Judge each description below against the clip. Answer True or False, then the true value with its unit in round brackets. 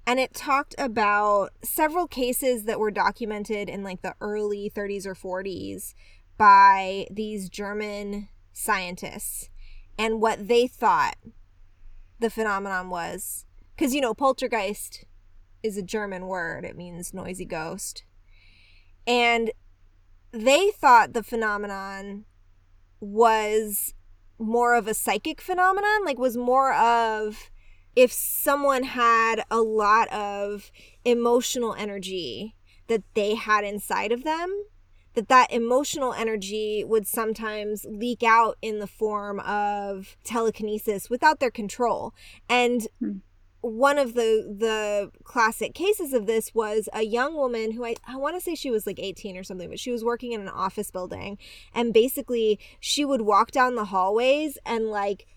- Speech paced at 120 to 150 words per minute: True (140 wpm)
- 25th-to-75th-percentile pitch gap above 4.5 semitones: False (3.8 semitones)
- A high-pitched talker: True (215 Hz)